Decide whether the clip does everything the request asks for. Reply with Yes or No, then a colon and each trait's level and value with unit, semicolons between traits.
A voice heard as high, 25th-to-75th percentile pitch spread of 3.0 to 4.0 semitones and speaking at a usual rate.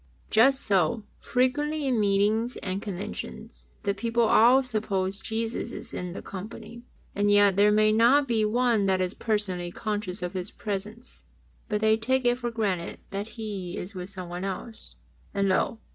Yes: high, 210 Hz; average, 3.3 semitones; average, 165 wpm